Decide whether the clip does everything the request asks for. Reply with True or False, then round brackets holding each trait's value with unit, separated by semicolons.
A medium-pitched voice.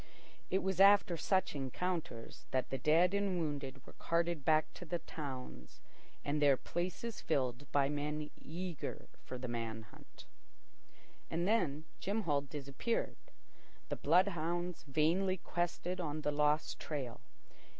True (155 Hz)